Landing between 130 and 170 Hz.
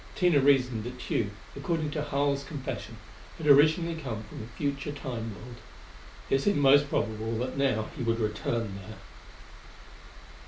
Yes: low, 135 Hz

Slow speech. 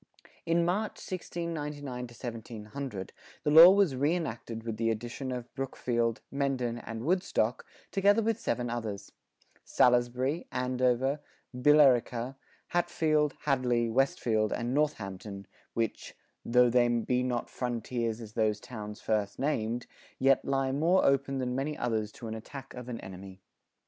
Yes: slow, 130 wpm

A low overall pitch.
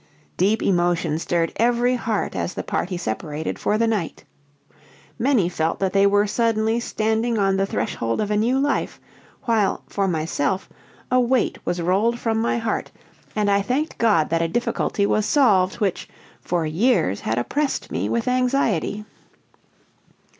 No: high, 205 Hz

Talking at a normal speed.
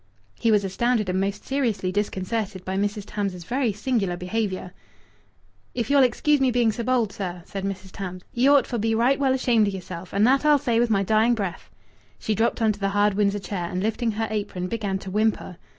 No: fast, 215 wpm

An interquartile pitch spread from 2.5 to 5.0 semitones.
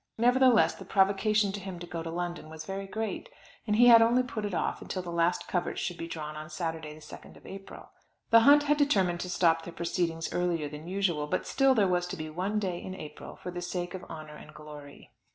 Yes: average, 4.1 semitones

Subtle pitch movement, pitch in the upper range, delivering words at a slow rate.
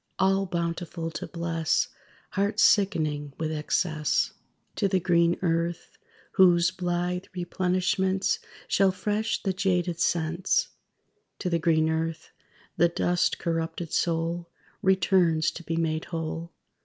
No: narrow, 2.1 semitones; medium, 170 Hz; slow, 120 wpm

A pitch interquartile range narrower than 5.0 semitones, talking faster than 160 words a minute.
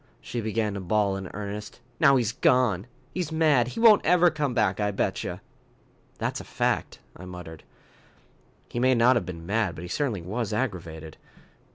No: wide, 5.5 semitones; average, 175 wpm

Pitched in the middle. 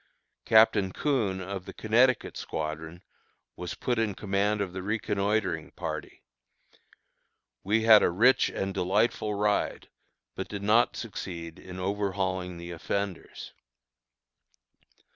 No: low, 100 Hz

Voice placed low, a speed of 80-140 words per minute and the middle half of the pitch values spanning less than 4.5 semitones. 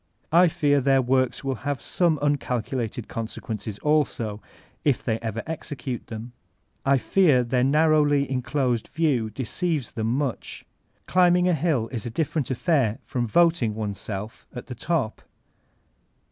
No: low, 130 Hz; slow, 135 wpm; average, 4.8 semitones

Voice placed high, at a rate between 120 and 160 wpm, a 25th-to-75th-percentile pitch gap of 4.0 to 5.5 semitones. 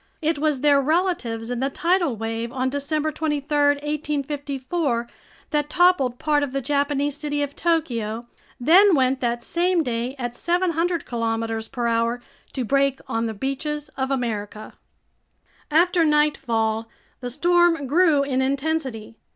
Yes: very high, 280 Hz; average, 140 wpm; average, 4.3 semitones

